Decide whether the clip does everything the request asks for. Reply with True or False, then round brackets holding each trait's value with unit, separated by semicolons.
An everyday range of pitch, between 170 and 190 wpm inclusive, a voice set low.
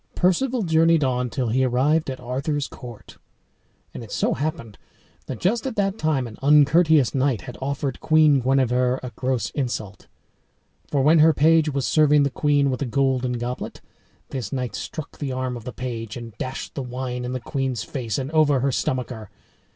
True (3.3 semitones; 180 wpm; 130 Hz)